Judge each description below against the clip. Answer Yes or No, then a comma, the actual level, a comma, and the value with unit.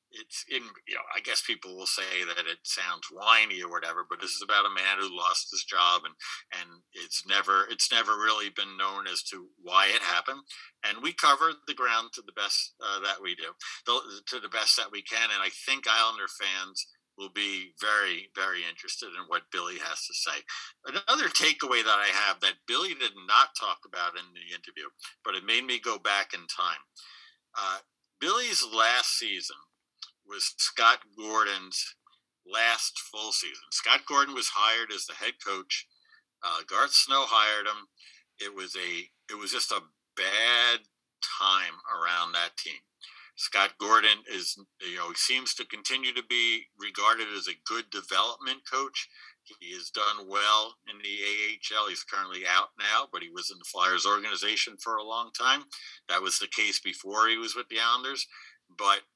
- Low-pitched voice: Yes, low, 110 Hz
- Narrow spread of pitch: No, average, 4.2 semitones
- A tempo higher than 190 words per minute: No, average, 185 wpm